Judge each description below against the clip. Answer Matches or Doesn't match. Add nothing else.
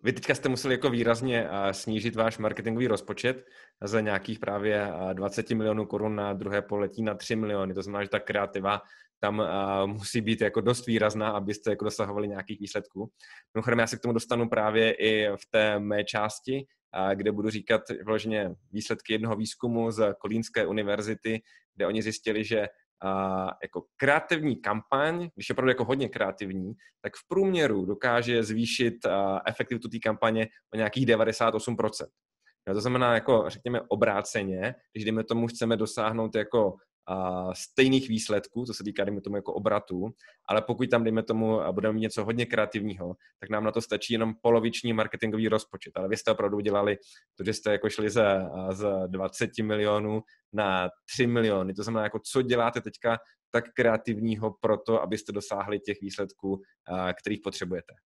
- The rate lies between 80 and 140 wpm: Doesn't match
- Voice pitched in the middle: Doesn't match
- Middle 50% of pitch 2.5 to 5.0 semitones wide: Doesn't match